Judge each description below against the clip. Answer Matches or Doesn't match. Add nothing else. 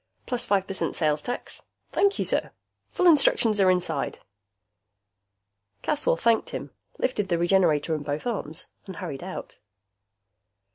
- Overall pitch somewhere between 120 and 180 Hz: Doesn't match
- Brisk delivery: Doesn't match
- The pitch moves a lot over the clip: Matches